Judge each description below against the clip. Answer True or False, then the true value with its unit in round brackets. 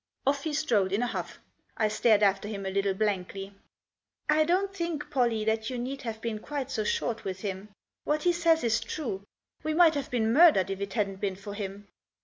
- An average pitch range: False (6.6 semitones)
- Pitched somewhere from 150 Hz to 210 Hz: False (220 Hz)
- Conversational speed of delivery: False (210 wpm)